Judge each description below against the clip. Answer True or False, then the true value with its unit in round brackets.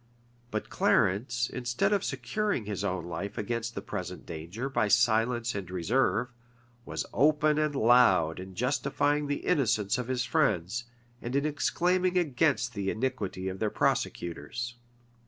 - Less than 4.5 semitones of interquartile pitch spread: False (5.5 semitones)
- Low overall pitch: True (120 Hz)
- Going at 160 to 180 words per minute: False (140 wpm)